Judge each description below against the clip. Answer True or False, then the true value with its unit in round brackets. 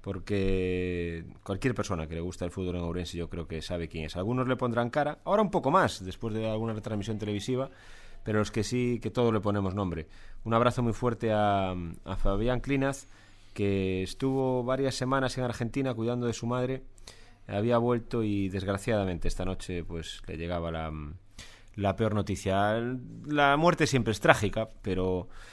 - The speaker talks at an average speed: True (180 wpm)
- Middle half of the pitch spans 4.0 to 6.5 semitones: True (4.8 semitones)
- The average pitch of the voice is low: True (105 Hz)